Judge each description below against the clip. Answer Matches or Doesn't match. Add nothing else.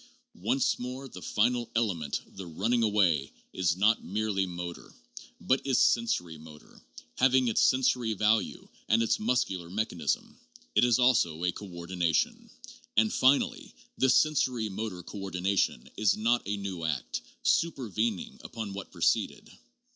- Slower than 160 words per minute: Matches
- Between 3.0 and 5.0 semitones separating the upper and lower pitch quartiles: Doesn't match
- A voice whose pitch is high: Doesn't match